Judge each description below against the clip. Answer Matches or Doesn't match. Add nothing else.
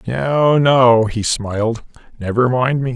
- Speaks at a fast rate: Doesn't match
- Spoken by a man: Matches